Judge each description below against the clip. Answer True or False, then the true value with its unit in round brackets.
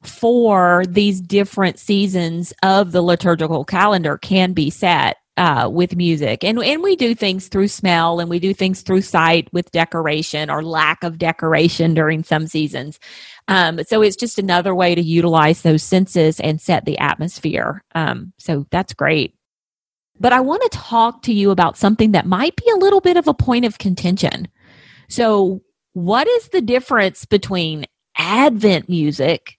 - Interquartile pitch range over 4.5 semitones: False (3.9 semitones)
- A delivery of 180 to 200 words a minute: False (165 wpm)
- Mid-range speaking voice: True (180 Hz)